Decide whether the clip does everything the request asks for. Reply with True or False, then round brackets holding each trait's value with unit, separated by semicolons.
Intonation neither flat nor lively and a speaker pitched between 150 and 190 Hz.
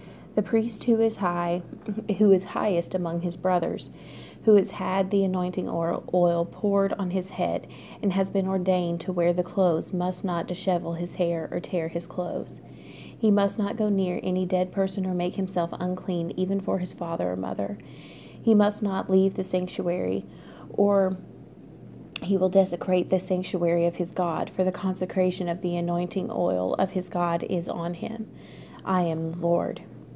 False (1.9 semitones; 185 Hz)